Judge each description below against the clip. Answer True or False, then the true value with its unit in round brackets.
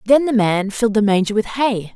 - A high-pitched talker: True (220 Hz)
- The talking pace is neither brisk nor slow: False (245 wpm)